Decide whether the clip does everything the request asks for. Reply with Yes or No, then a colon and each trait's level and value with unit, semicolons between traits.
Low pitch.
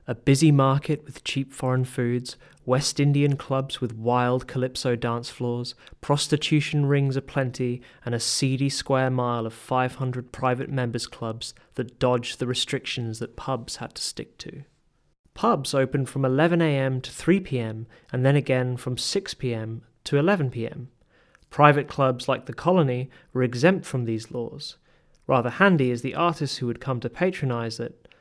Yes: low, 130 Hz